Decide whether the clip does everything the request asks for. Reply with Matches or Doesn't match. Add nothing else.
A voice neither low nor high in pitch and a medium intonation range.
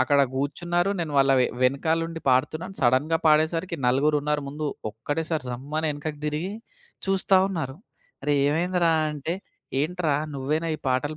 Matches